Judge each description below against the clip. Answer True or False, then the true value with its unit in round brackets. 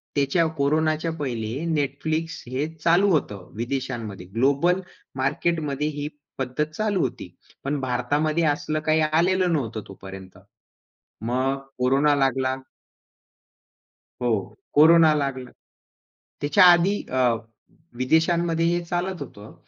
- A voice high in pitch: False (145 Hz)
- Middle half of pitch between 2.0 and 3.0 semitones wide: False (4.1 semitones)